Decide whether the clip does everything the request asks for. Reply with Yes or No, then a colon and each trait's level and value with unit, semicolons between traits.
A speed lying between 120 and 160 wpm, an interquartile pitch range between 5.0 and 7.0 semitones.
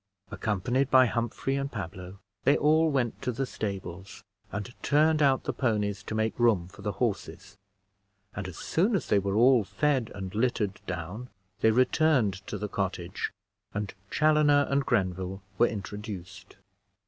Yes: average, 155 wpm; average, 5.3 semitones